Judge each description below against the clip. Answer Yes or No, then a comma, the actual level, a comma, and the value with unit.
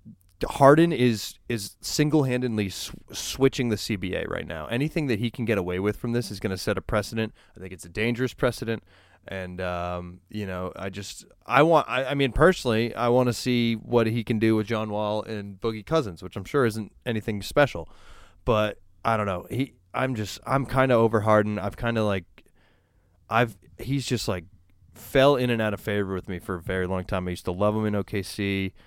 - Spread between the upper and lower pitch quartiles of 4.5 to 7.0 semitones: No, average, 3.8 semitones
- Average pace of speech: No, fast, 215 wpm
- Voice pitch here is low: Yes, low, 110 Hz